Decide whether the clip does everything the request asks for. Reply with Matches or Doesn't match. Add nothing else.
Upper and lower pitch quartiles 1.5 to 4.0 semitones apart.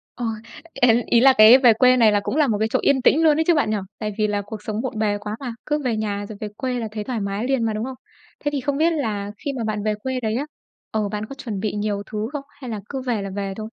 Matches